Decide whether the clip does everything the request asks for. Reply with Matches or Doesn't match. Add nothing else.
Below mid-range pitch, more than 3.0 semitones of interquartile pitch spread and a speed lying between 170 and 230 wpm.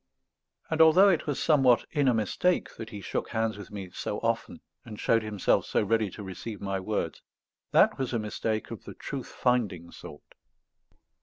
Matches